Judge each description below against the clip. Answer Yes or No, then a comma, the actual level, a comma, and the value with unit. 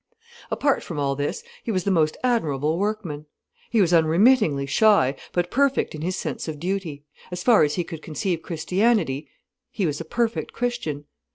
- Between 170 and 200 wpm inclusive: Yes, average, 175 wpm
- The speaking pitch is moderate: Yes, medium, 175 Hz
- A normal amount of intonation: No, wide, 6.2 semitones